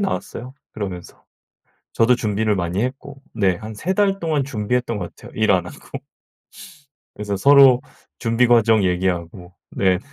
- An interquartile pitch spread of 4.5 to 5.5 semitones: Yes, average, 5.2 semitones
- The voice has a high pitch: No, low, 110 Hz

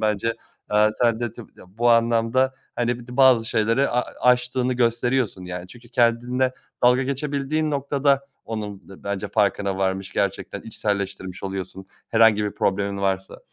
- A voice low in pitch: Yes, low, 115 Hz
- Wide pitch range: No, average, 3.9 semitones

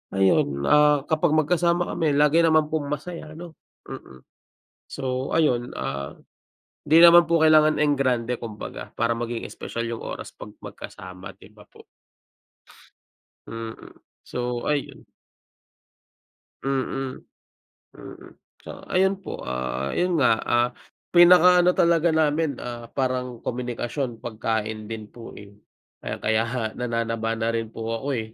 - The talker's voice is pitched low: Yes, low, 125 Hz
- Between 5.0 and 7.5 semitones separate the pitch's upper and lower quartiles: Yes, wide, 5.5 semitones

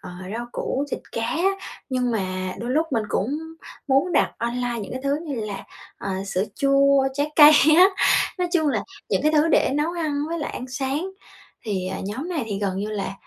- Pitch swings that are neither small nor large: No, wide, 5.9 semitones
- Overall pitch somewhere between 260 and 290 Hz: Yes, very high, 265 Hz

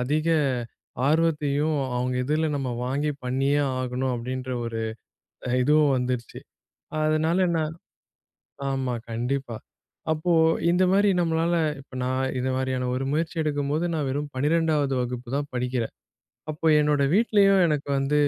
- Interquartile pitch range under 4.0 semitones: Yes, average, 3.4 semitones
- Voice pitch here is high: No, medium, 145 Hz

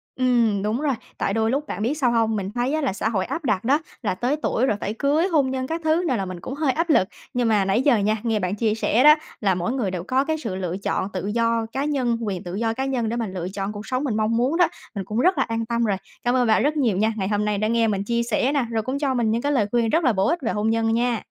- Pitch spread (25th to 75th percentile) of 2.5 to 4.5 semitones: Yes, average, 4.0 semitones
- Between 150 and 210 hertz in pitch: No, high, 230 Hz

